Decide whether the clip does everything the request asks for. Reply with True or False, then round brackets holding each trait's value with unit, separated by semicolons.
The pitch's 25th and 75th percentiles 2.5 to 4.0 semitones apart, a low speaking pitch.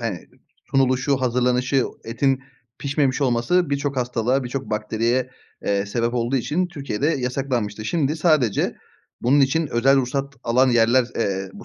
True (2.9 semitones; 130 Hz)